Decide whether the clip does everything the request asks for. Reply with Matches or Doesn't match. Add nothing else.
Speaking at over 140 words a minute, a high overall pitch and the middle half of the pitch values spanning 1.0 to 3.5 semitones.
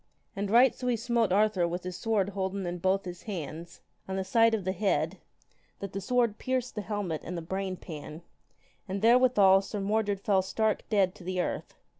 Matches